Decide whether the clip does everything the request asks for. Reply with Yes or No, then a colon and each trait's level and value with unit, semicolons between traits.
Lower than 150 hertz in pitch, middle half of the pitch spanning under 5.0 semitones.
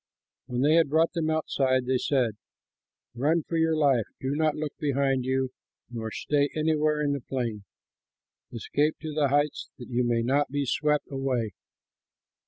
Yes: medium, 140 Hz; average, 3.1 semitones